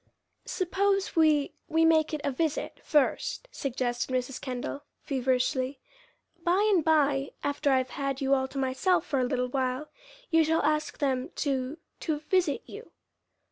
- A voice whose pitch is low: No, very high, 285 Hz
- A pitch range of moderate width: Yes, average, 3.5 semitones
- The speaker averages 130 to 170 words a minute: Yes, average, 150 wpm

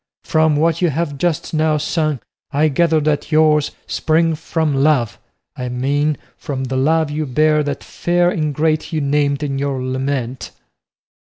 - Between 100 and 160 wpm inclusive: Yes, average, 155 wpm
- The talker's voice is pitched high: No, medium, 150 Hz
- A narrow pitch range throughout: Yes, narrow, 2.2 semitones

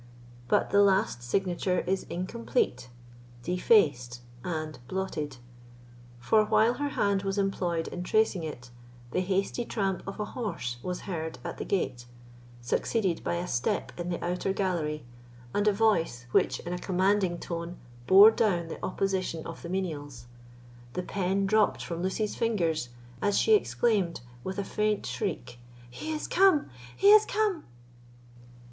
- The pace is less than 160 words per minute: Yes, average, 145 wpm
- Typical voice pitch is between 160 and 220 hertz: Yes, medium, 185 Hz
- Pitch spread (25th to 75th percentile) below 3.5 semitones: No, average, 3.9 semitones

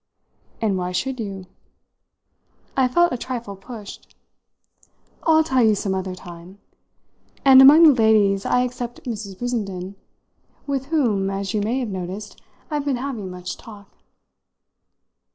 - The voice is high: Yes, high, 220 Hz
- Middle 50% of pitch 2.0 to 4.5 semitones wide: No, average, 4.9 semitones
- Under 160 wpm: Yes, average, 140 wpm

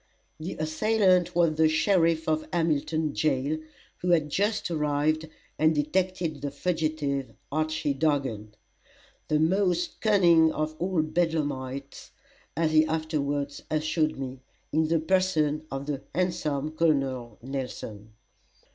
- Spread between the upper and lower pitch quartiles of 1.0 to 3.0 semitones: Yes, average, 2.7 semitones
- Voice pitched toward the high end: No, medium, 155 Hz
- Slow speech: Yes, slow, 120 wpm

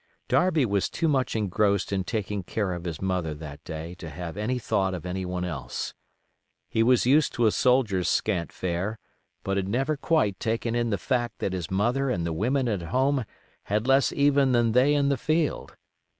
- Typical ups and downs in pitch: No, wide, 5.9 semitones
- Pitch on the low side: Yes, low, 105 Hz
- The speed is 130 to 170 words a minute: No, average, 195 wpm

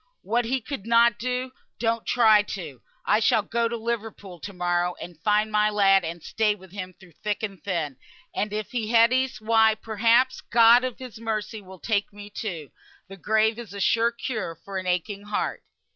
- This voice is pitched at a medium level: No, high, 215 Hz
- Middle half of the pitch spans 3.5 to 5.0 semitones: No, average, 2.9 semitones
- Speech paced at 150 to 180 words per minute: No, average, 190 wpm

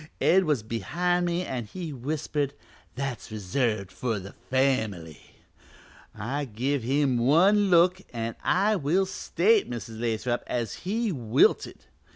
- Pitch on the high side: No, low, 135 Hz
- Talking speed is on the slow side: Yes, slow, 130 wpm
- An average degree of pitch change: No, wide, 7.3 semitones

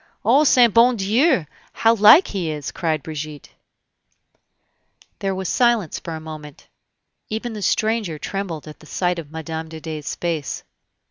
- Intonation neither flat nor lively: No, wide, 5.8 semitones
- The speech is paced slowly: No, average, 150 wpm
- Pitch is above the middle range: No, medium, 175 Hz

